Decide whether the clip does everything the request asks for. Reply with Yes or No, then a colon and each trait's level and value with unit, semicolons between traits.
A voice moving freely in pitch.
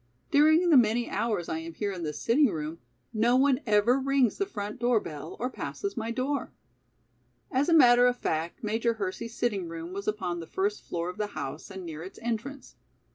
Yes: wide, 6.1 semitones